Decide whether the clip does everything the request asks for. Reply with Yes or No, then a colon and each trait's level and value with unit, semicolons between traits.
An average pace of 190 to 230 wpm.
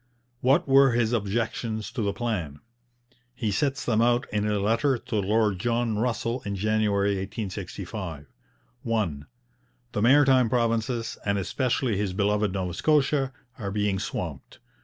No: average, 140 wpm